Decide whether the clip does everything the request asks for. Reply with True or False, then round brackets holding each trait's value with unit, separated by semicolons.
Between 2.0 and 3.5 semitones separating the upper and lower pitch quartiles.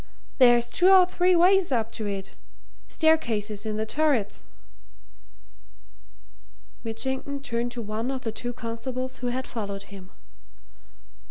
False (4.2 semitones)